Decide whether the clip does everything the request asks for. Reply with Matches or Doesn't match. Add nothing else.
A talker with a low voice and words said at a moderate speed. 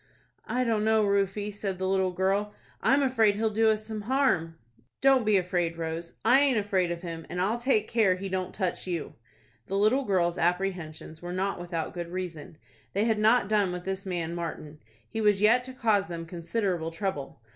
Doesn't match